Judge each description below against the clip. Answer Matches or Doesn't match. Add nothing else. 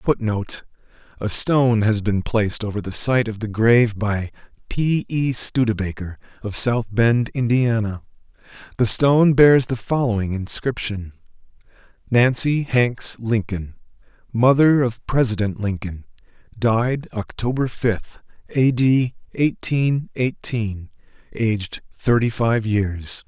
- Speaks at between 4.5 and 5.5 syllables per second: Doesn't match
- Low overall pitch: Matches